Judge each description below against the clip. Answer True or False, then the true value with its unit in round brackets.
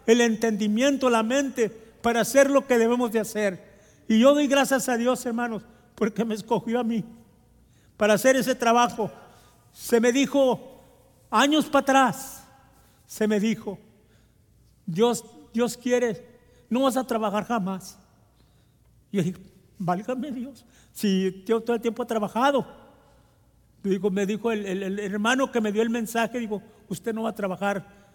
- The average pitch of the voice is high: True (225 Hz)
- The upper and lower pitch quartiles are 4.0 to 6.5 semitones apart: False (3.2 semitones)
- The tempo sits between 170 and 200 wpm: False (160 wpm)